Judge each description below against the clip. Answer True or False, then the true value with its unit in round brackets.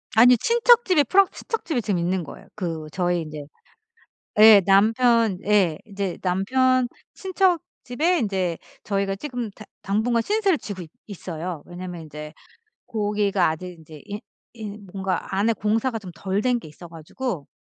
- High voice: True (205 Hz)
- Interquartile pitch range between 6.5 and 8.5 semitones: False (5.4 semitones)